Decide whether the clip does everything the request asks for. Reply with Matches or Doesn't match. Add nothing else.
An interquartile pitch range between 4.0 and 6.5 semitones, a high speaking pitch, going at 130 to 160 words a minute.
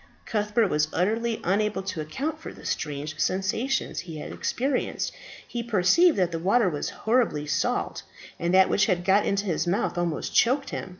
Doesn't match